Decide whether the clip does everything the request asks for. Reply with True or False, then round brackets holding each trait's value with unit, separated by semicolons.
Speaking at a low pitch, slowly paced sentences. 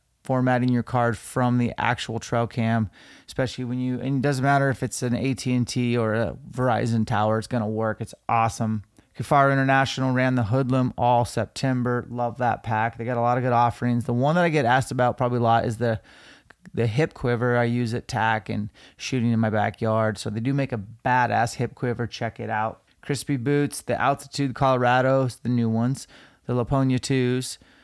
False (120 Hz; 200 wpm)